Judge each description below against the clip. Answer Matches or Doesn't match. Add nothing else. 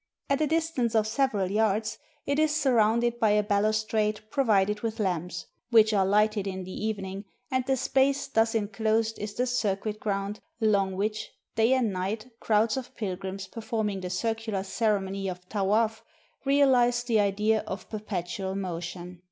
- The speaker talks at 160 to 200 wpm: Matches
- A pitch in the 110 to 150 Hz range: Doesn't match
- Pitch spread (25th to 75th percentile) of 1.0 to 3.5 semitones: Matches